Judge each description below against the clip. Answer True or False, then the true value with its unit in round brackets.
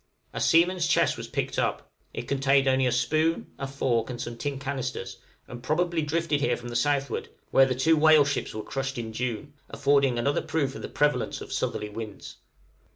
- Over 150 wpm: True (195 wpm)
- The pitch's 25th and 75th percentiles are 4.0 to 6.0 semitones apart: False (3.3 semitones)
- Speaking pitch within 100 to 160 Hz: True (135 Hz)